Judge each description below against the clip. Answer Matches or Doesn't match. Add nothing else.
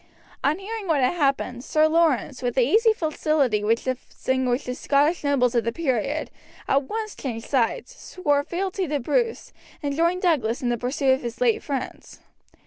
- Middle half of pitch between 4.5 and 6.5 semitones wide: Matches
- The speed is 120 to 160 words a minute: Doesn't match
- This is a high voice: Matches